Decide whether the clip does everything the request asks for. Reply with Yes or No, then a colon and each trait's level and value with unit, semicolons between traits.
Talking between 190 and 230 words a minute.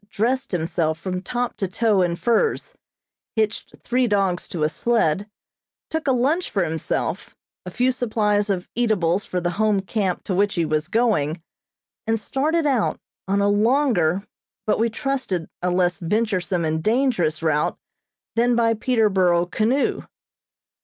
No: average, 150 wpm